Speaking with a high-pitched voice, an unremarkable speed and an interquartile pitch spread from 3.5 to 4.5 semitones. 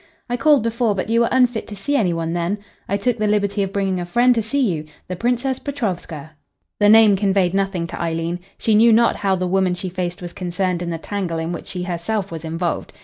No: high, 195 Hz; fast, 235 wpm; average, 4.2 semitones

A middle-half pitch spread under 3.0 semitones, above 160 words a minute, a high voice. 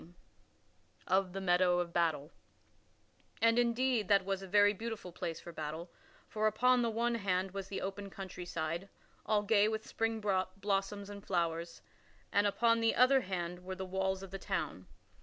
No: average, 3.3 semitones; average, 170 wpm; high, 195 Hz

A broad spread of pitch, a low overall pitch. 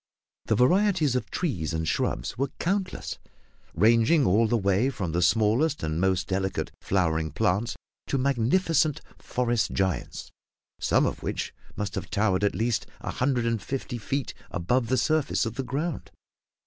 Yes: wide, 6.2 semitones; low, 115 Hz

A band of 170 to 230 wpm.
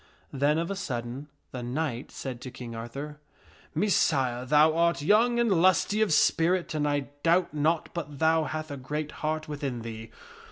Yes: average, 175 wpm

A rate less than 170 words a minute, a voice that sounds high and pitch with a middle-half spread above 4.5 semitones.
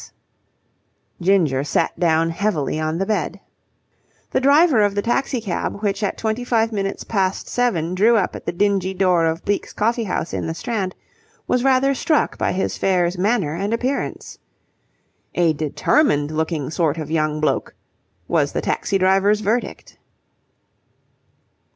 Yes: average, 150 wpm; high, 195 Hz; average, 5.2 semitones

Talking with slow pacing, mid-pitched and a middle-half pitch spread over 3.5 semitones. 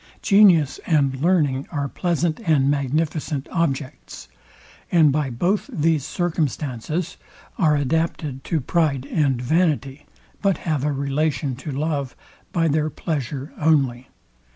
No: slow, 120 wpm; medium, 150 Hz; average, 3.1 semitones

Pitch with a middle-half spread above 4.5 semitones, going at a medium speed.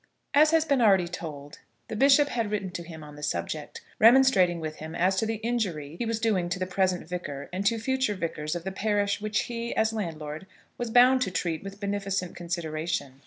No: average, 5.0 semitones; fast, 210 wpm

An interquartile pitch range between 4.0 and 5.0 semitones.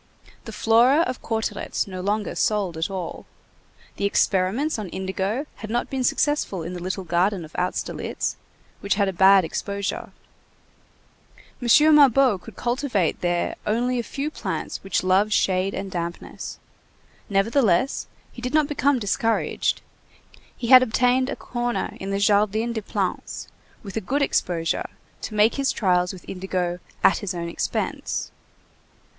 Yes: average, 4.6 semitones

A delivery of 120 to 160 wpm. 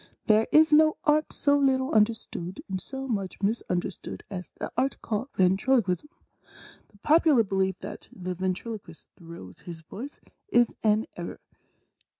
Yes: average, 145 wpm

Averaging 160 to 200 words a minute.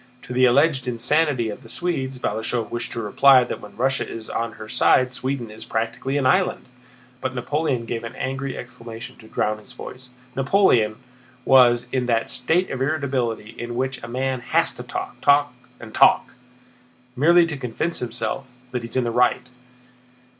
Yes: average, 175 wpm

